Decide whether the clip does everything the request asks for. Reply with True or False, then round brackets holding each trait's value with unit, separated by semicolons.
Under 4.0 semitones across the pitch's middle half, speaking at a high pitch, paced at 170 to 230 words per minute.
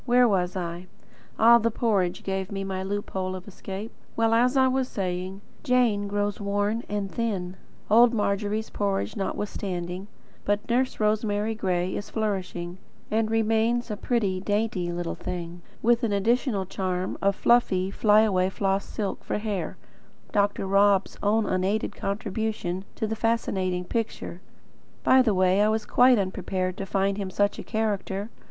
False (2.8 semitones; 205 Hz; 155 wpm)